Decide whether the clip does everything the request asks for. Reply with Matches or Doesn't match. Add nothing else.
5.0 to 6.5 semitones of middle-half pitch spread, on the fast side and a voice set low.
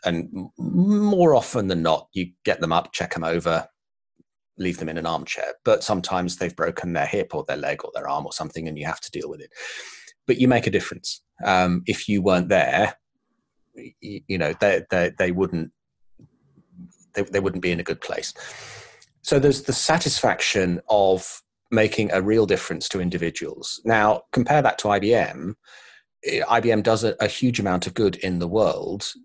Doesn't match